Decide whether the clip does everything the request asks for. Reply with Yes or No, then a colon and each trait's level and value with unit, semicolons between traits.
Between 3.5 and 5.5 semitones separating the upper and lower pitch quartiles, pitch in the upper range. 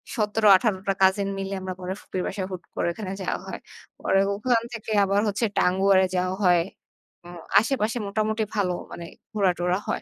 No: narrow, 2.4 semitones; high, 195 Hz